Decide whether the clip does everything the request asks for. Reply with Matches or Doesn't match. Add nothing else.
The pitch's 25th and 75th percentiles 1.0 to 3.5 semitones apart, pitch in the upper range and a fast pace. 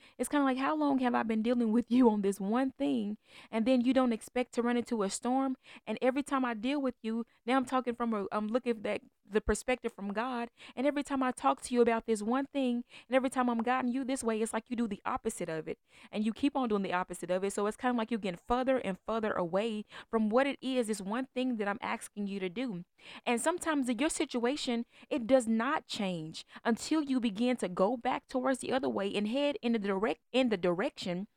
Matches